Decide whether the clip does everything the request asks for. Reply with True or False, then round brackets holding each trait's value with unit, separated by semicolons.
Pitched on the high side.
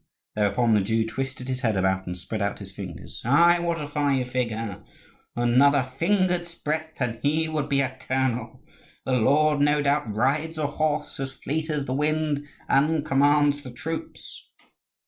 False (140 Hz)